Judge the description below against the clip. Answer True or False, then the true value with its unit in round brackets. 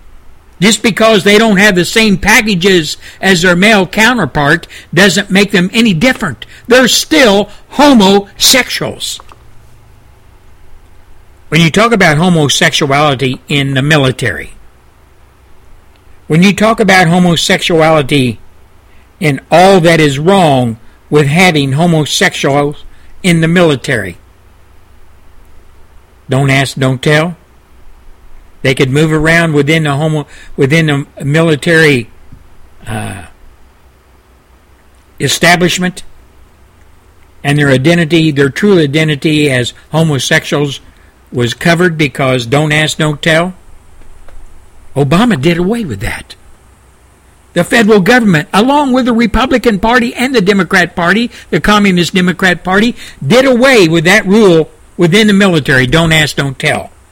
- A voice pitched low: False (150 Hz)